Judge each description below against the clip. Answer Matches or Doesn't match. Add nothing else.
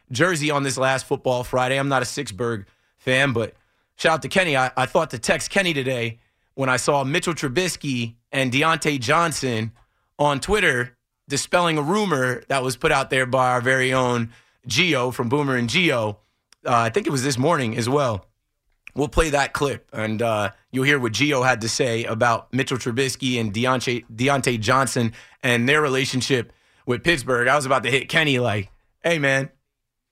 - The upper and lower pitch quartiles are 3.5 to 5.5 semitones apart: Doesn't match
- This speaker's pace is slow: Doesn't match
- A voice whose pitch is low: Matches